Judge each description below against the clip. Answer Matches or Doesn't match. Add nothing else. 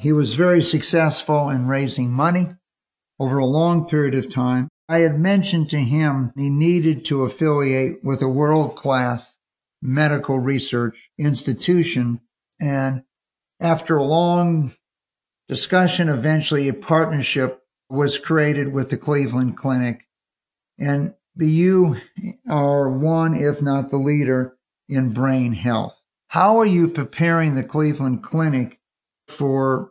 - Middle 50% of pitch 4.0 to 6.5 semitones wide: Doesn't match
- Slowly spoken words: Matches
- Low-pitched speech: Doesn't match